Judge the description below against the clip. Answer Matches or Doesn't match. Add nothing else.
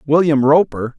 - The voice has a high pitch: Doesn't match